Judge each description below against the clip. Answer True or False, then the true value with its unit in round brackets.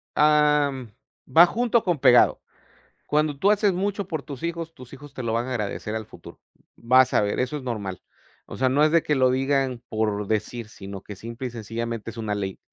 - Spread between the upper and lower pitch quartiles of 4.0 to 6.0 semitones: True (5.2 semitones)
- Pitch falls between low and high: False (130 Hz)